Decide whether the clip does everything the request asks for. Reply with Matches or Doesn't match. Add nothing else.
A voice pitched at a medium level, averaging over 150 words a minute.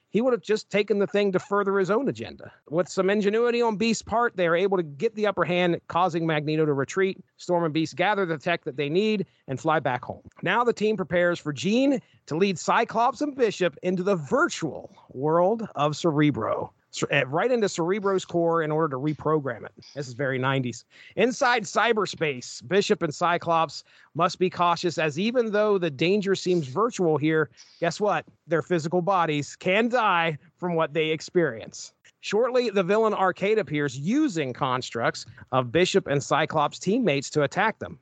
Matches